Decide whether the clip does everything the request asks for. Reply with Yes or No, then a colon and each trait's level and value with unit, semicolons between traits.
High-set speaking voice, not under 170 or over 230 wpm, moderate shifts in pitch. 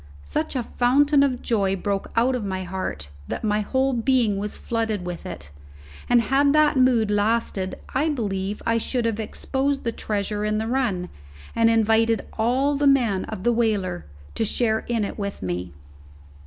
Yes: high, 225 Hz; average, 175 wpm; average, 4.0 semitones